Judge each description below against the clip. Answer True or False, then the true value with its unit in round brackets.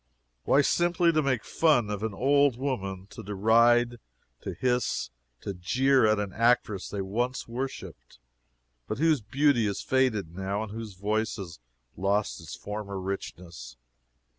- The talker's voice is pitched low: True (110 Hz)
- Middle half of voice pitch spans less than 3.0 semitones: False (4.8 semitones)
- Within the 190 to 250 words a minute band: False (145 wpm)